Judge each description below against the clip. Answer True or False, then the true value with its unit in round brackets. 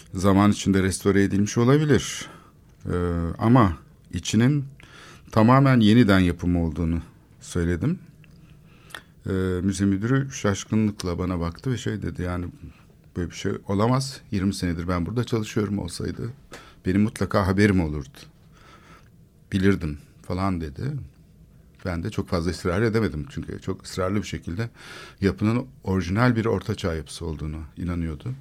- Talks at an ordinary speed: True (125 wpm)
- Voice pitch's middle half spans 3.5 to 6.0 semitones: True (4.5 semitones)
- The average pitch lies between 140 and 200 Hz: False (100 Hz)